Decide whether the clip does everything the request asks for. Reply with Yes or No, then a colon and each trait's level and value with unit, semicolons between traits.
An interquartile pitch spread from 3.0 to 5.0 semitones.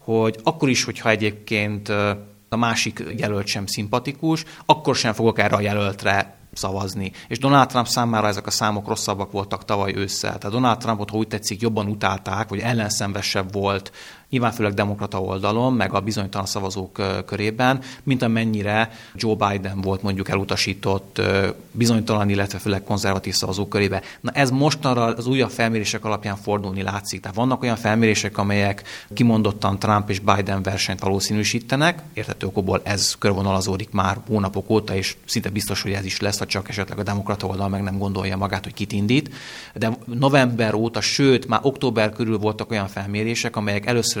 No: narrow, 2.6 semitones